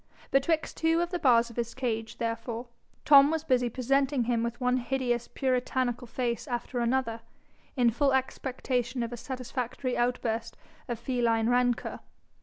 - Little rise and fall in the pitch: Yes, narrow, 2.0 semitones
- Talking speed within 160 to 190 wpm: No, average, 150 wpm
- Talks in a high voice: Yes, high, 245 Hz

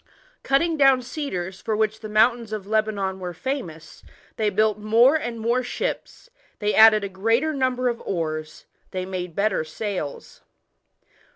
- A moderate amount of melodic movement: Yes, average, 4.5 semitones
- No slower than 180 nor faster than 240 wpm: No, average, 150 wpm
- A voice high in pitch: Yes, high, 215 Hz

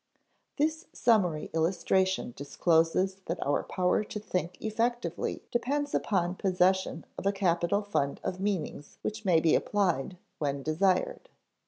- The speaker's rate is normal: No, slow, 130 wpm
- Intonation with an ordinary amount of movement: Yes, average, 3.9 semitones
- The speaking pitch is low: No, medium, 185 Hz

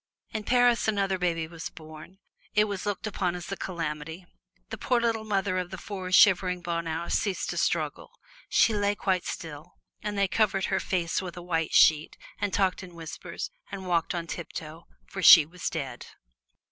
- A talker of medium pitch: Yes, medium, 180 Hz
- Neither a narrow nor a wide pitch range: Yes, average, 3.3 semitones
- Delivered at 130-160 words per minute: No, average, 185 wpm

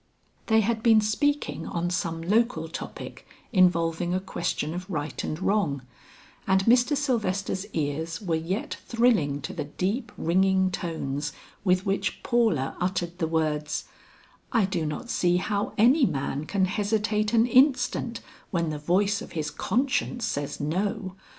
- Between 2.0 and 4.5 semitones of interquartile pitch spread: No, average, 5.1 semitones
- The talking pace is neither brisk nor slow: Yes, average, 145 wpm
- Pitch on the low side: No, medium, 185 Hz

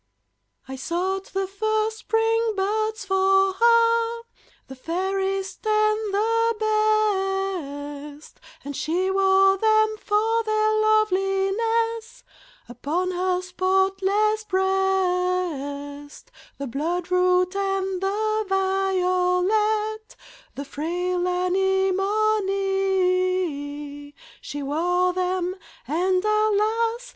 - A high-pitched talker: Yes, very high, 385 Hz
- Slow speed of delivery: Yes, slow, 85 wpm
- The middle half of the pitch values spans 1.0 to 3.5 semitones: Yes, average, 3.0 semitones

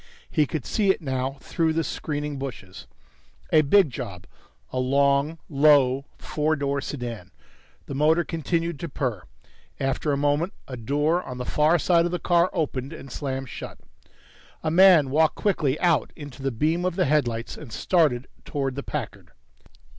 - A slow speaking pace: No, average, 165 wpm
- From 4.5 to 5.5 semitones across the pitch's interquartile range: No, average, 3.5 semitones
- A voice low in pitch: No, medium, 145 Hz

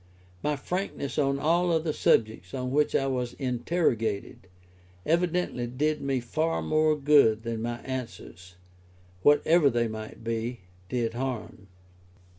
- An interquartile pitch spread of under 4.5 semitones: No, average, 4.8 semitones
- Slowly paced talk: Yes, slow, 125 wpm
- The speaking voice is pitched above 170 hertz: No, low, 130 Hz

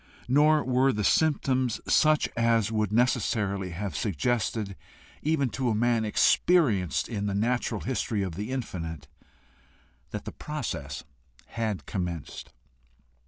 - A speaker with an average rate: No, slow, 120 wpm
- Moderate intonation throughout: Yes, average, 4.5 semitones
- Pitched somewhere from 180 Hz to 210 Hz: No, low, 110 Hz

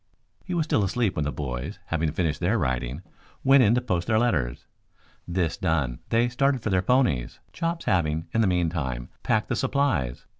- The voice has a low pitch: Yes, very low, 90 Hz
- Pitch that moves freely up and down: Yes, wide, 8.2 semitones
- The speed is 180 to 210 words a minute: Yes, average, 185 wpm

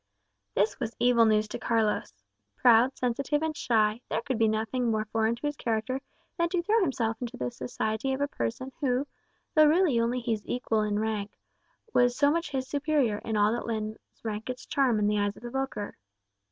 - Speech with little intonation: No, average, 3.7 semitones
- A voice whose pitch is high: Yes, high, 235 Hz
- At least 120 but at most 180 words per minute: No, average, 200 wpm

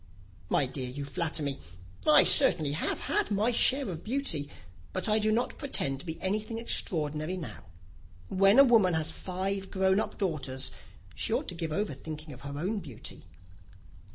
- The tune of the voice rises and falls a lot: Yes, wide, 6.2 semitones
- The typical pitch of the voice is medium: Yes, medium, 180 Hz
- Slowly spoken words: No, average, 175 wpm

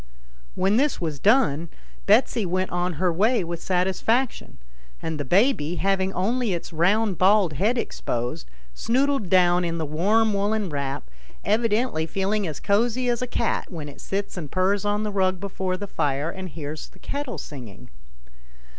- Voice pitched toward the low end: No, high, 190 Hz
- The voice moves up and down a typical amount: Yes, average, 4.5 semitones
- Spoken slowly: No, average, 165 wpm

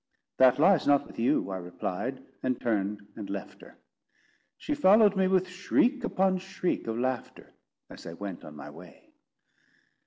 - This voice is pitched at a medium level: No, low, 130 Hz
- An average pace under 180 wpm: Yes, average, 160 wpm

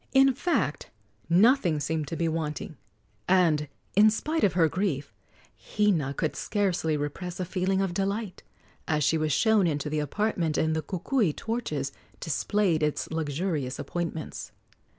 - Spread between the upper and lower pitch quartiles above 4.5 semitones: Yes, average, 4.9 semitones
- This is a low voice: No, medium, 170 Hz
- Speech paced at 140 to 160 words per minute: Yes, average, 145 wpm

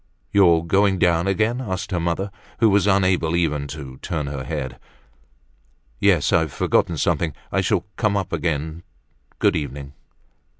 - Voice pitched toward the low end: Yes, very low, 85 Hz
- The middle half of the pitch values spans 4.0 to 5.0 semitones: Yes, average, 4.3 semitones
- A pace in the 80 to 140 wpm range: No, average, 155 wpm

